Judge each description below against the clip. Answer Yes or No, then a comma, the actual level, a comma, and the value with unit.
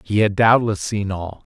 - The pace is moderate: Yes, average, 195 wpm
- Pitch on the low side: Yes, low, 105 Hz